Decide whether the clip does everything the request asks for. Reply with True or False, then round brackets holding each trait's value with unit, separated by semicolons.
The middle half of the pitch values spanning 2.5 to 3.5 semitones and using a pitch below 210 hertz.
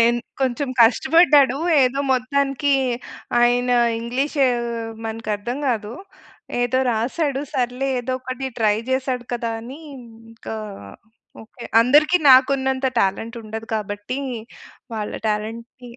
False (2.8 semitones; 245 Hz)